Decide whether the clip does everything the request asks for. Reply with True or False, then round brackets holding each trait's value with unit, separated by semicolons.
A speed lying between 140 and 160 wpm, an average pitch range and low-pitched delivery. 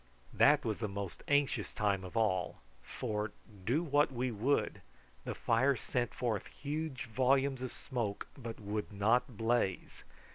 True (145 wpm; 4.2 semitones; 120 Hz)